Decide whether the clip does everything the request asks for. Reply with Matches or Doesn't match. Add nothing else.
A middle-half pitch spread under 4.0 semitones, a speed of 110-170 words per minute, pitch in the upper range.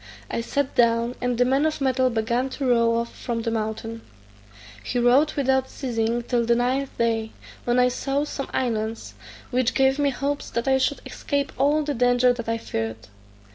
Doesn't match